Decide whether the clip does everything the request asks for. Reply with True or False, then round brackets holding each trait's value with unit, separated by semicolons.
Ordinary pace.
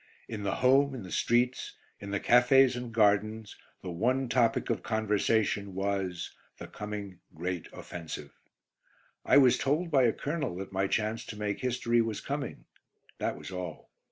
True (160 wpm)